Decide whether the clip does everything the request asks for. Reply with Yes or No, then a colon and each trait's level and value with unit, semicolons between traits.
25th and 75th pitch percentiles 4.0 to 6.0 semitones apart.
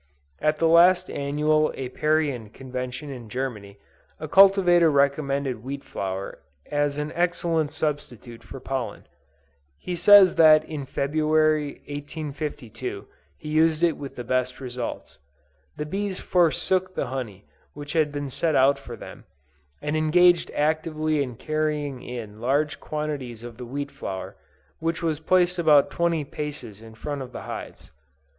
No: average, 3.6 semitones